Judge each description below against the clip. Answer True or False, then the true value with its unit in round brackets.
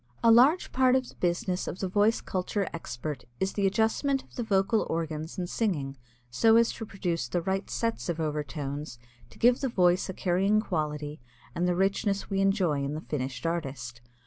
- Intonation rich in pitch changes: True (5.8 semitones)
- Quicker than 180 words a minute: True (190 wpm)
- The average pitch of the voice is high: False (180 Hz)